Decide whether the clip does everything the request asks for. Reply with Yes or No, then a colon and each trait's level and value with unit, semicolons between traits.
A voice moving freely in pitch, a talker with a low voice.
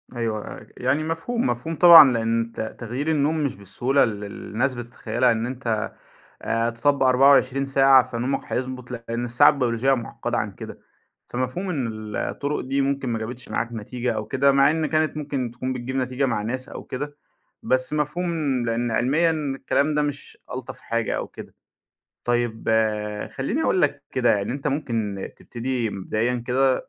No: average, 3.1 semitones; low, 130 Hz